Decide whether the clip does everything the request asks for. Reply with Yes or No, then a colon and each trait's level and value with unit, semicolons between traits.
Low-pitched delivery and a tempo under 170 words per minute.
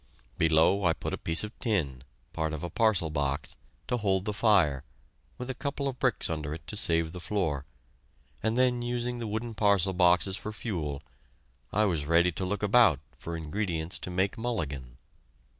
No: very low, 95 Hz; average, 180 wpm